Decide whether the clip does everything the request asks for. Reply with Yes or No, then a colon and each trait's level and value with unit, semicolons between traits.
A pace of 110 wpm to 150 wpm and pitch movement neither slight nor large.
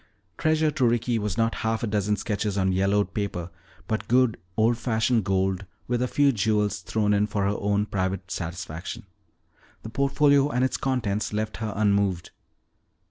No: average, 165 wpm; average, 3.1 semitones